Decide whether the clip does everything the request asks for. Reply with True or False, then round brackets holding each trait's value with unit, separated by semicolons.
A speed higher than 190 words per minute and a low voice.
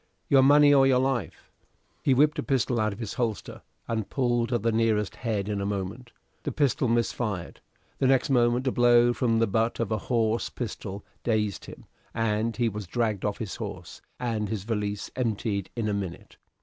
True (200 wpm; 115 Hz)